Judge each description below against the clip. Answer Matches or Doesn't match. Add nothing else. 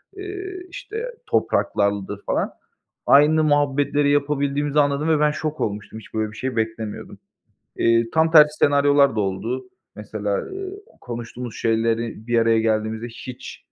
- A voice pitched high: Doesn't match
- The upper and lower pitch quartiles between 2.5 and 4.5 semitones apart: Doesn't match